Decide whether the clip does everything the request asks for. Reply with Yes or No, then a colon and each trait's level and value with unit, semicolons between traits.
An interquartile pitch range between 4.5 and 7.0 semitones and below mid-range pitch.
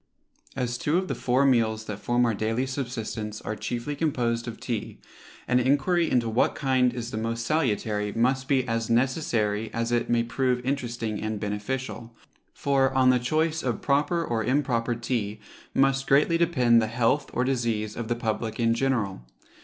No: average, 2.8 semitones; low, 120 Hz